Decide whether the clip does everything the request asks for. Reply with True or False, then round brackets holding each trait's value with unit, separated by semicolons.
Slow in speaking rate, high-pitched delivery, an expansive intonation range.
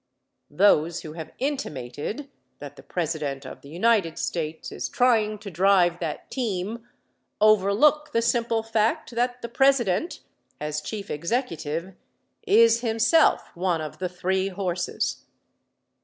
True (125 wpm; 195 Hz; 5.9 semitones)